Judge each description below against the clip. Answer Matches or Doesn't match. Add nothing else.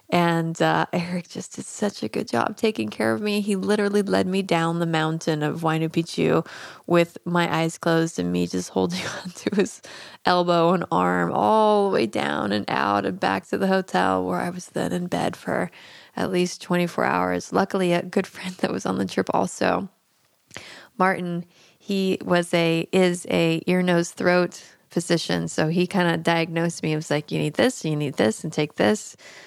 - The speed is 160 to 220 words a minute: Matches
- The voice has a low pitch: Doesn't match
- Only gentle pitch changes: Doesn't match